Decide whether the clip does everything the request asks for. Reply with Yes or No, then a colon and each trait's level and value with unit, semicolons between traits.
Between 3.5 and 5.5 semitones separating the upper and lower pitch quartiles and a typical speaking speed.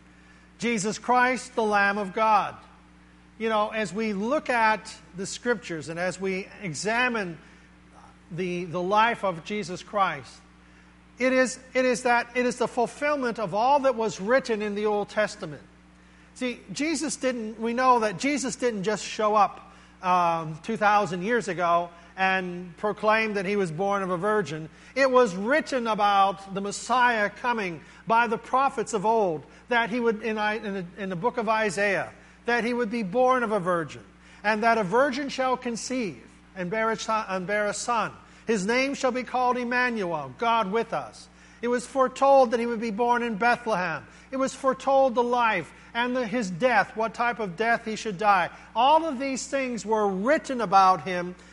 Yes: average, 4.3 semitones; average, 175 wpm